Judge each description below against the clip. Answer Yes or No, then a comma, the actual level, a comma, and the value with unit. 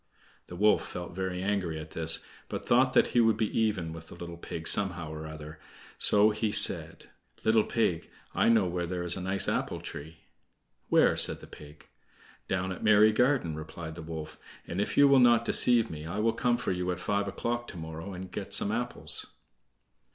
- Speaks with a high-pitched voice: No, very low, 90 Hz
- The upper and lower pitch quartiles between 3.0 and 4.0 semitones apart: No, average, 4.9 semitones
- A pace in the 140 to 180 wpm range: No, average, 200 wpm